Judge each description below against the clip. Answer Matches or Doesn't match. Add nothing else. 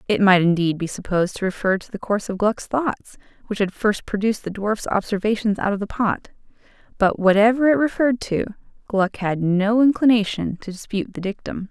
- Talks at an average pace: Matches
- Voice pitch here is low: Doesn't match